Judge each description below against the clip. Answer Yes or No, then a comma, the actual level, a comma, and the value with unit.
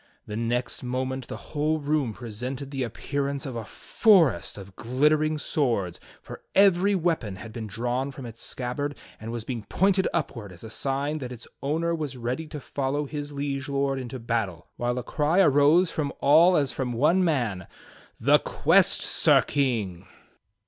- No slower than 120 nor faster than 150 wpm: No, average, 170 wpm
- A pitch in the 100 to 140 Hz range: Yes, low, 135 Hz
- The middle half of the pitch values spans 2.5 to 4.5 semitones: Yes, average, 4.2 semitones